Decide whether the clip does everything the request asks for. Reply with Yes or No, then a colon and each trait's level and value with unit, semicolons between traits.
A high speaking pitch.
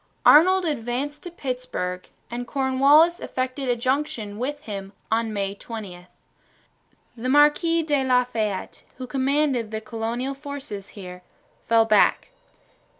Yes: very high, 250 Hz